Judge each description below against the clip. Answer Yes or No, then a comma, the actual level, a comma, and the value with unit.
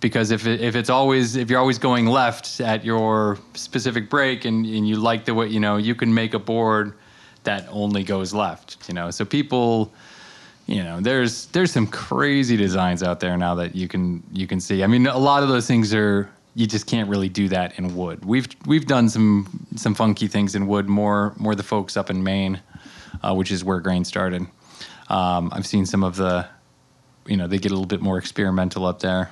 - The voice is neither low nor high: No, low, 105 Hz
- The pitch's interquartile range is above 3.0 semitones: Yes, average, 3.5 semitones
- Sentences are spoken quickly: Yes, fast, 220 wpm